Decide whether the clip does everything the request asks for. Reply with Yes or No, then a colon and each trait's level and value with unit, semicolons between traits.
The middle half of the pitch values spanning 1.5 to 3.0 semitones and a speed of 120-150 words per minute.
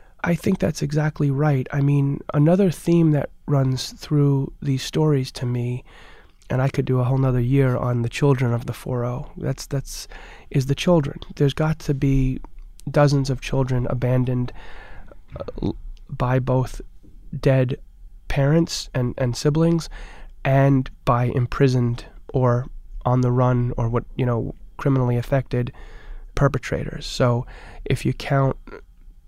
Yes: narrow, 2.5 semitones; average, 140 wpm